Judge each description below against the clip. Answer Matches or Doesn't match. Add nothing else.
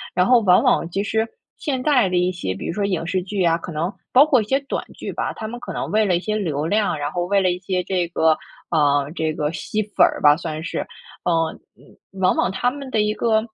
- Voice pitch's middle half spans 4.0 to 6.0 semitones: Matches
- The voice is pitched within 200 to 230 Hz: Doesn't match